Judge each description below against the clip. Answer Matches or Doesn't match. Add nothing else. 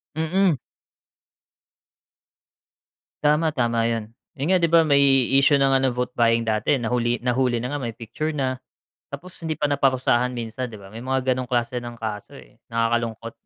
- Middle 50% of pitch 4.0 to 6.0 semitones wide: Doesn't match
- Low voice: Matches